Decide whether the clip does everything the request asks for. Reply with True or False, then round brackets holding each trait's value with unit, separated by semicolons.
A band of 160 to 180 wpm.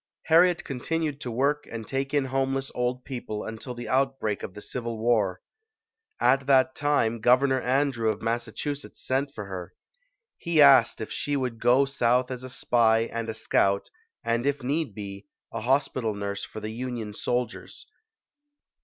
True (165 wpm)